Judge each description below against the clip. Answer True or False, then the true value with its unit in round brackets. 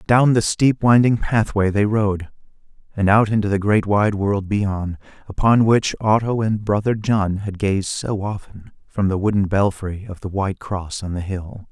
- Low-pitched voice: True (100 Hz)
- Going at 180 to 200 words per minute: True (185 wpm)